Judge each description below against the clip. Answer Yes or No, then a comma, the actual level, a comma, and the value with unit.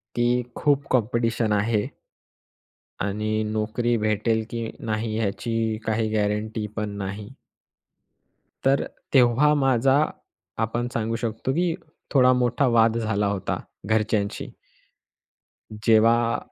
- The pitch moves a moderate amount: No, narrow, 2.0 semitones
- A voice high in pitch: No, low, 115 Hz